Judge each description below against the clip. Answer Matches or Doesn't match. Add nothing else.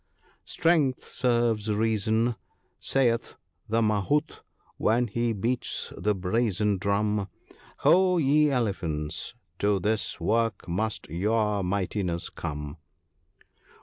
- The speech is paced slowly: Matches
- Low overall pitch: Matches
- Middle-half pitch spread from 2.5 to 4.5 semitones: Matches